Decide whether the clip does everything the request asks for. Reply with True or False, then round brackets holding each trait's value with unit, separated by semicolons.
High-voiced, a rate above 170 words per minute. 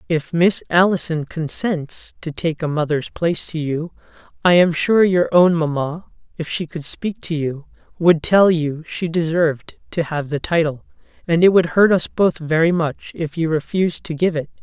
False (165 Hz; 190 wpm)